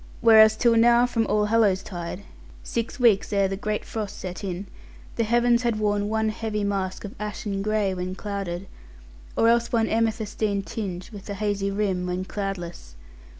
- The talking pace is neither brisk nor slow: Yes, average, 165 wpm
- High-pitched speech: Yes, high, 210 Hz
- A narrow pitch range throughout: Yes, narrow, 2.3 semitones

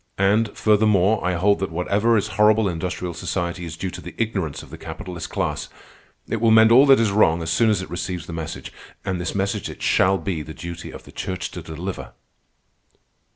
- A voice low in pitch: Yes, very low, 95 Hz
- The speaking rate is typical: No, fast, 210 wpm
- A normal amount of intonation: Yes, average, 3.7 semitones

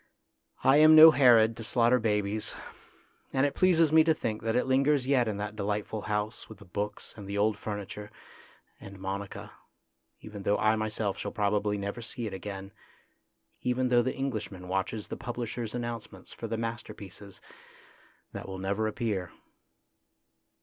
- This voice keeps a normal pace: Yes, average, 165 wpm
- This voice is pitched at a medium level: No, low, 110 Hz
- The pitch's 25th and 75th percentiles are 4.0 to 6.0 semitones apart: No, average, 3.1 semitones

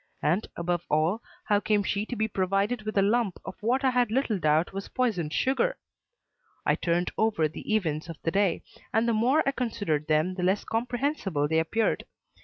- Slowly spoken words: No, average, 195 wpm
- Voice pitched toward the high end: Yes, high, 205 Hz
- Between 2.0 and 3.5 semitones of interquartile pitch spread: No, average, 5.3 semitones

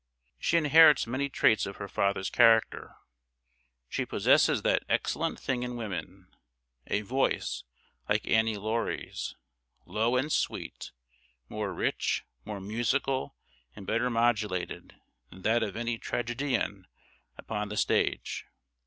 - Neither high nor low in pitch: No, low, 115 Hz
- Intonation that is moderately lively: Yes, average, 3.4 semitones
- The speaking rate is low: Yes, slow, 120 wpm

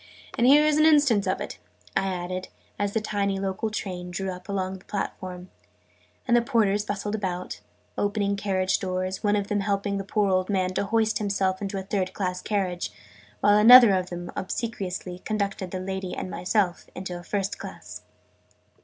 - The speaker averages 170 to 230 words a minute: Yes, average, 180 wpm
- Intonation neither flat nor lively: No, narrow, 2.0 semitones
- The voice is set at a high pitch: Yes, high, 195 Hz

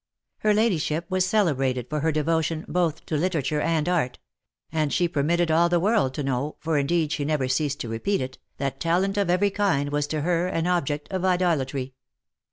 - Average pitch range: Yes, average, 3.8 semitones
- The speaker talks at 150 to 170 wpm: No, average, 190 wpm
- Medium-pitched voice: Yes, medium, 160 Hz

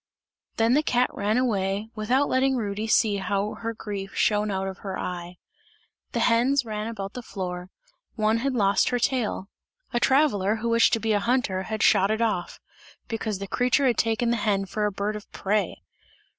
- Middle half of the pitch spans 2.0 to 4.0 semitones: Yes, average, 3.1 semitones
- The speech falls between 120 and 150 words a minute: No, average, 190 wpm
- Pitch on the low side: No, high, 215 Hz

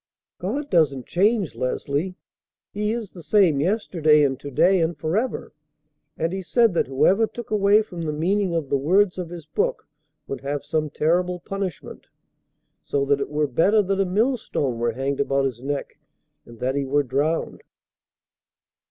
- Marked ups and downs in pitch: Yes, wide, 5.8 semitones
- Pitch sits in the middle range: Yes, medium, 165 Hz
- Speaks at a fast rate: No, average, 170 wpm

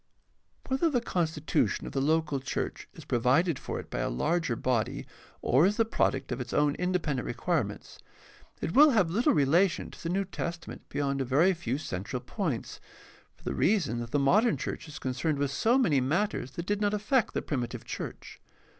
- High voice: No, medium, 160 Hz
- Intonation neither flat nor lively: No, wide, 6.6 semitones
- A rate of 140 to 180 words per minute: No, average, 190 wpm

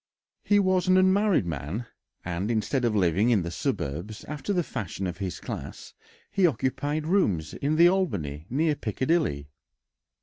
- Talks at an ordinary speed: Yes, average, 155 wpm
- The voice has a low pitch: Yes, low, 125 Hz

